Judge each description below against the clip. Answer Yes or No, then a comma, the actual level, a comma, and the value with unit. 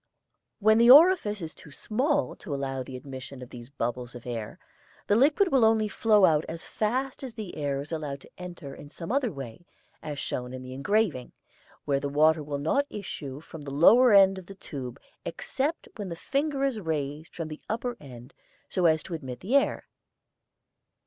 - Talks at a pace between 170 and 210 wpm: Yes, average, 195 wpm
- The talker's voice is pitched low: No, medium, 160 Hz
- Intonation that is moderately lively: No, wide, 8.0 semitones